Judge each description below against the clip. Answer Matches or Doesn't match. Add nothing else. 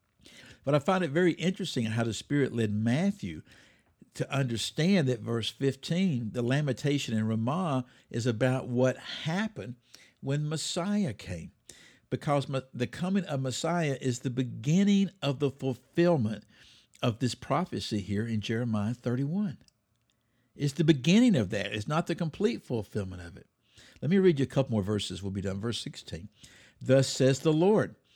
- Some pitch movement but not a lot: Doesn't match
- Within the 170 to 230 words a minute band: Doesn't match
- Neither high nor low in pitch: Doesn't match